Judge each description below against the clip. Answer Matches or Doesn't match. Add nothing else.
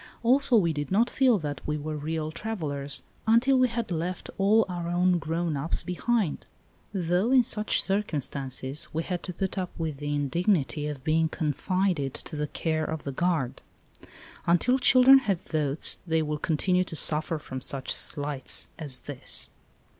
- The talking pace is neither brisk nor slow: Matches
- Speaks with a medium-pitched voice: Matches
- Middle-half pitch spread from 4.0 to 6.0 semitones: Matches